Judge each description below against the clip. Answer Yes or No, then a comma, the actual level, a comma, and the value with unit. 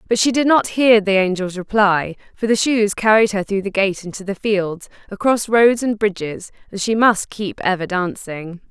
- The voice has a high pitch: Yes, high, 205 Hz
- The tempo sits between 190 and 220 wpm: Yes, average, 200 wpm